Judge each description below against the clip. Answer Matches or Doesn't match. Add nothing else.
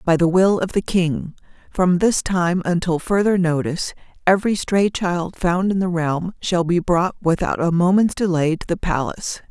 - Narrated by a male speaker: Doesn't match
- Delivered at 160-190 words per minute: Matches